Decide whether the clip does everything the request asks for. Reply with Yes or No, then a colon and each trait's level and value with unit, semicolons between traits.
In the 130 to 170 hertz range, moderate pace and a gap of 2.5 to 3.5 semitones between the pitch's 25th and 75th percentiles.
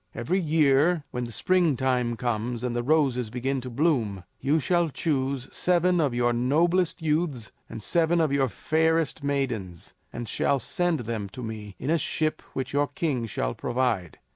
No: low, 135 Hz; average, 165 wpm; average, 5.0 semitones